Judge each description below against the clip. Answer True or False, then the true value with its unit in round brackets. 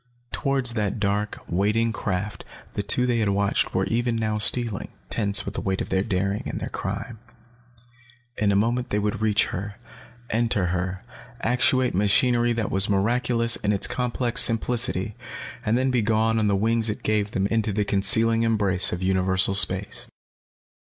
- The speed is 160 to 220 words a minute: True (170 wpm)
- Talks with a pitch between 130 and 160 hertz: False (105 Hz)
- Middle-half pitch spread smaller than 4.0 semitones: True (2.7 semitones)